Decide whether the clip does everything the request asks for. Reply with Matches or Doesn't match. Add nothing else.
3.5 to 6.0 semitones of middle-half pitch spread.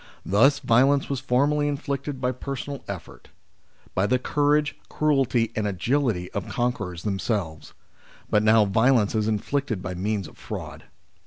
Matches